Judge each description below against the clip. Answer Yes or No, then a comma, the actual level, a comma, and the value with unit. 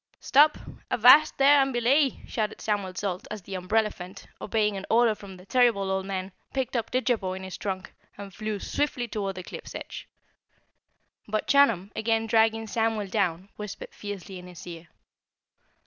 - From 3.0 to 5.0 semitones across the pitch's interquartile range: Yes, average, 3.6 semitones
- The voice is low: No, high, 210 Hz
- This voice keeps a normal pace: Yes, average, 165 wpm